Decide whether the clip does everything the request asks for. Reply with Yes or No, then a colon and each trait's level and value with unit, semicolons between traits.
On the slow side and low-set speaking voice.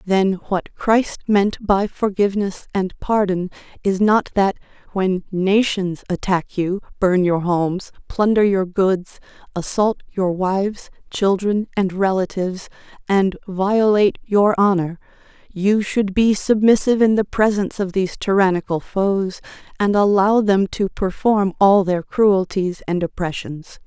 No: slow, 130 wpm; high, 195 Hz